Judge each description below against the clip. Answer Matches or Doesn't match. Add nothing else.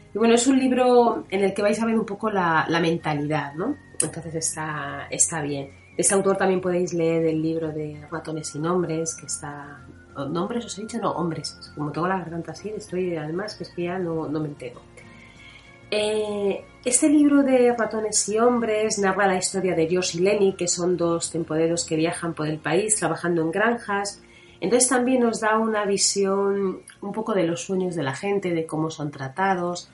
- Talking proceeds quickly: Matches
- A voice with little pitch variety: Doesn't match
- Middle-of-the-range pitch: Matches